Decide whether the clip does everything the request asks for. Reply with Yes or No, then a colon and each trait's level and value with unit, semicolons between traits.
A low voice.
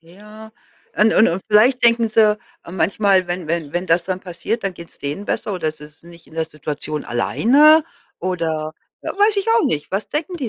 No: medium, 185 Hz